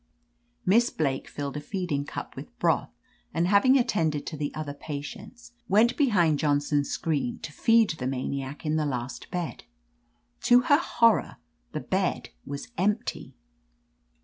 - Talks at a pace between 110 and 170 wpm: Yes, average, 145 wpm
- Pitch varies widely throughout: Yes, wide, 6.7 semitones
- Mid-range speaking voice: Yes, medium, 155 Hz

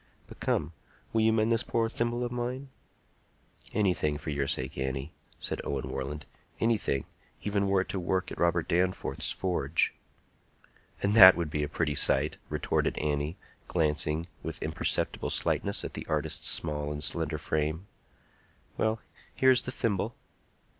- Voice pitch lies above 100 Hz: No, very low, 85 Hz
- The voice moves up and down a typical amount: No, wide, 6.7 semitones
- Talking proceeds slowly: No, average, 150 wpm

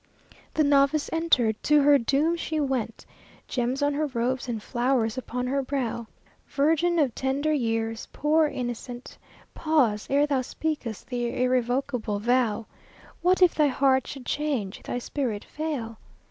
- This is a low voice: No, very high, 265 Hz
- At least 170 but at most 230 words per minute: No, average, 145 wpm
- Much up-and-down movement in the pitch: No, average, 3.6 semitones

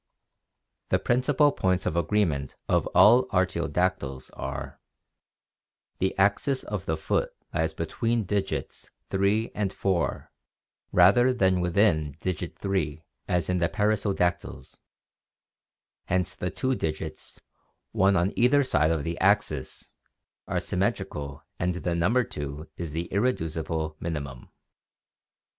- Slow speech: Yes, slow, 115 wpm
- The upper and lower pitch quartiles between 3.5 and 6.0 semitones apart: Yes, average, 4.5 semitones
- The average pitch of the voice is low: Yes, very low, 90 Hz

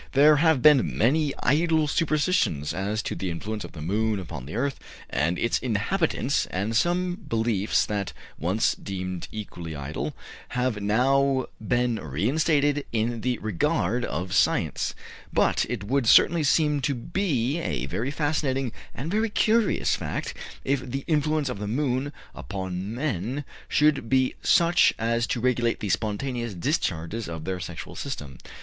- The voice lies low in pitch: Yes, low, 120 Hz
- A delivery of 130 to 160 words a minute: Yes, average, 150 wpm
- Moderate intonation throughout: No, wide, 6.3 semitones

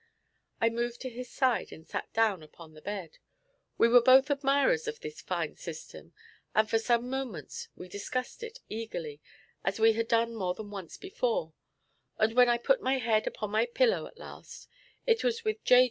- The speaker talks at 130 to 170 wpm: No, average, 190 wpm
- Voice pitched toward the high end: Yes, high, 235 Hz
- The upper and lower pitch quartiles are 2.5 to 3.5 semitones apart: No, average, 4.4 semitones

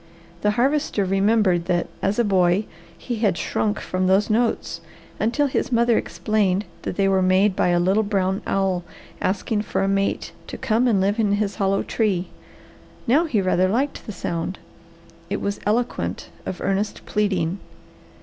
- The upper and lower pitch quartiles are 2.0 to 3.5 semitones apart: Yes, narrow, 2.6 semitones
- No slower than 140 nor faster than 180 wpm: Yes, average, 165 wpm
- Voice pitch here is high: Yes, high, 200 Hz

